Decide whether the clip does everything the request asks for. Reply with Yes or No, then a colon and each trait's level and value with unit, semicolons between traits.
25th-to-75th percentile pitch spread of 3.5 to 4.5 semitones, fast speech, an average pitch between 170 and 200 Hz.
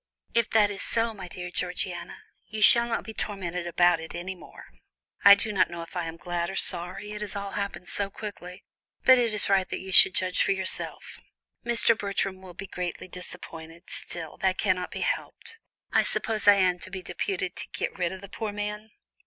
No: average, 2.7 semitones; fast, 210 wpm; high, 190 Hz